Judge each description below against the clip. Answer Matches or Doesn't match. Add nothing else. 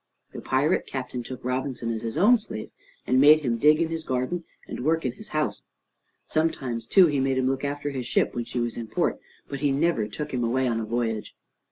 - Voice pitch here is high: Doesn't match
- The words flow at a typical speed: Doesn't match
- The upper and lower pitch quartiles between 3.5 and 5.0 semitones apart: Matches